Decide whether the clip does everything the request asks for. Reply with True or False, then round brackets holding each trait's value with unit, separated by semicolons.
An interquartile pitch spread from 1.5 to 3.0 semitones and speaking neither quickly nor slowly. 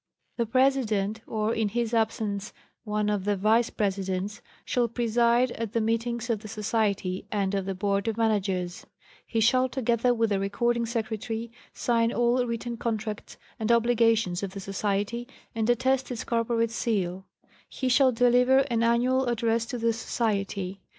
True (2.5 semitones; 155 wpm)